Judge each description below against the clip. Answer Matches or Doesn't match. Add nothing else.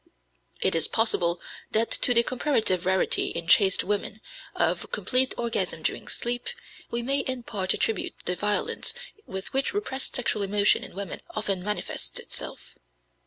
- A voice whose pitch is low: Doesn't match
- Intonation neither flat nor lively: Matches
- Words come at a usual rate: Matches